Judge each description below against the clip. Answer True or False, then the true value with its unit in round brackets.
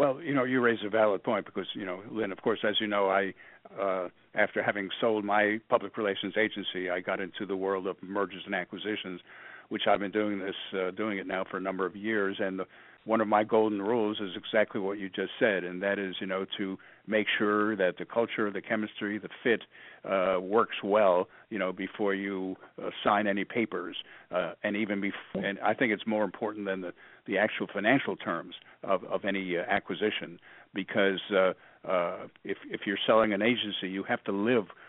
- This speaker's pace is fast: True (210 wpm)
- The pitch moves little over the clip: True (1.9 semitones)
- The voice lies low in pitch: True (100 Hz)